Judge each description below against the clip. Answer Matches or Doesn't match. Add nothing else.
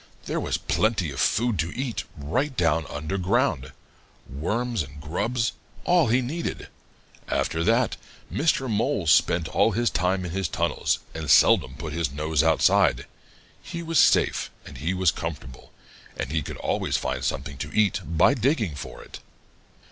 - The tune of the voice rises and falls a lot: Matches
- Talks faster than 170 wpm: Doesn't match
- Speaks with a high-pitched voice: Doesn't match